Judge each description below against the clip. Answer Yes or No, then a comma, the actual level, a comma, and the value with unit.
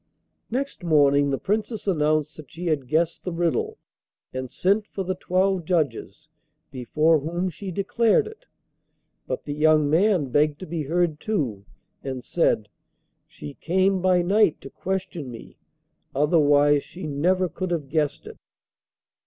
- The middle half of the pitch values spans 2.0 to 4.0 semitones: No, average, 4.4 semitones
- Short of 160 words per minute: Yes, average, 145 wpm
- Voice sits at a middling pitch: Yes, medium, 165 Hz